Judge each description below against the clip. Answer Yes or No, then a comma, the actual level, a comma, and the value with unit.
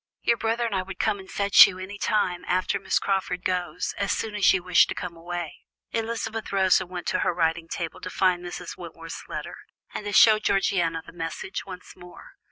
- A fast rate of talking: Yes, fast, 210 wpm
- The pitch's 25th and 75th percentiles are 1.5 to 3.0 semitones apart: Yes, narrow, 2.4 semitones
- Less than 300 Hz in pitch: Yes, medium, 185 Hz